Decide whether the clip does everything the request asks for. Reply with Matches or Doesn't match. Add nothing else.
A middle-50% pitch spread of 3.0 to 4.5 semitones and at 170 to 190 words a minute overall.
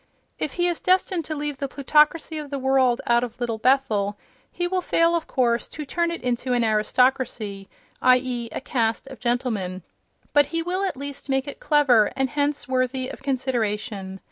Matches